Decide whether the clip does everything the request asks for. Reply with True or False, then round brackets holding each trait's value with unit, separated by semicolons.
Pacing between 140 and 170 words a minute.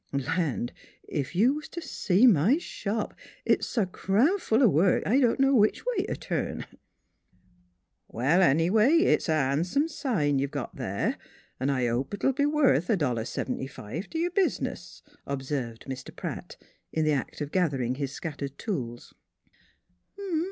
True (165 wpm)